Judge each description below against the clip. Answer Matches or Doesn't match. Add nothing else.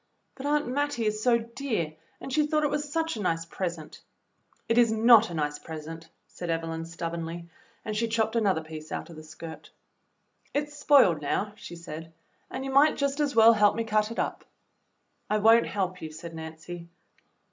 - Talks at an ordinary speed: Matches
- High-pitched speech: Matches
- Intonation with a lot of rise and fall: Matches